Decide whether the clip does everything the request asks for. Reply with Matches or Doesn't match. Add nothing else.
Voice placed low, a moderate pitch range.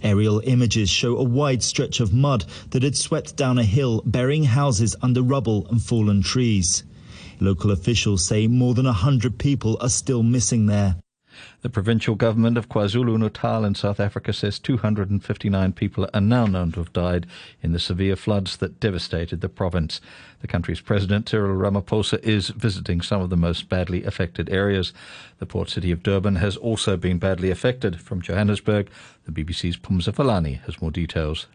Matches